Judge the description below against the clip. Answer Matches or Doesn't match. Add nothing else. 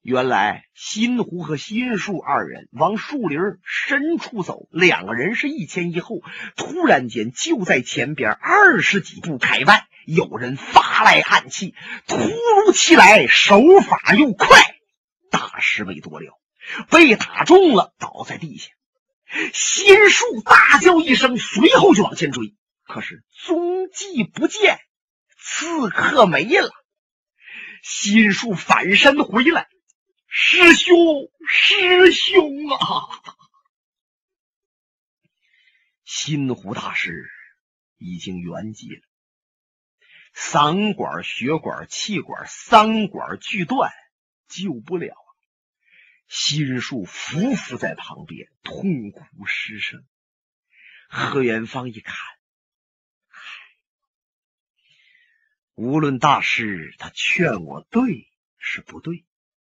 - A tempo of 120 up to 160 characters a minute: Matches